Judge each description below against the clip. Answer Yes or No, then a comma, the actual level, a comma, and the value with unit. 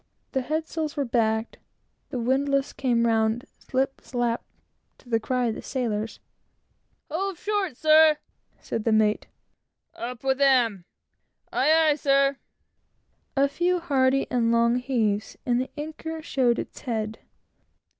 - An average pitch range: Yes, average, 3.9 semitones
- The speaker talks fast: No, slow, 135 wpm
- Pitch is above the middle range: Yes, very high, 260 Hz